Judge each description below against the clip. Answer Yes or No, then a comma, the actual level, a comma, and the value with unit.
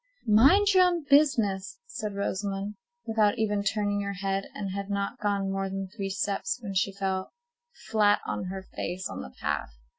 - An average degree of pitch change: No, narrow, 2.2 semitones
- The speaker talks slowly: No, average, 175 wpm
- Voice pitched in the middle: No, high, 200 Hz